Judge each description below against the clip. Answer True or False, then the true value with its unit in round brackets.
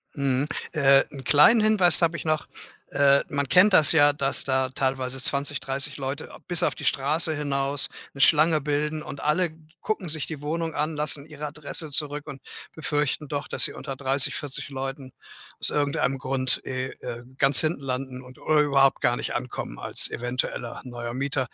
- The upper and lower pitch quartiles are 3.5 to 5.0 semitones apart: False (2.4 semitones)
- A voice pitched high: False (140 Hz)